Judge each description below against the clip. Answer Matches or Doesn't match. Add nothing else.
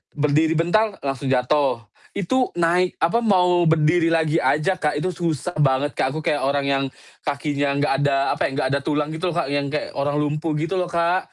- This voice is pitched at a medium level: Matches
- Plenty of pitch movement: Doesn't match